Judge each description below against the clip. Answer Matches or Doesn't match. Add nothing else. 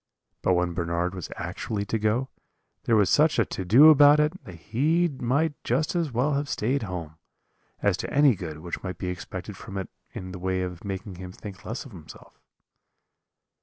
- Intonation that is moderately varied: Doesn't match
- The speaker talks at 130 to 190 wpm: Doesn't match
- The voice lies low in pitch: Matches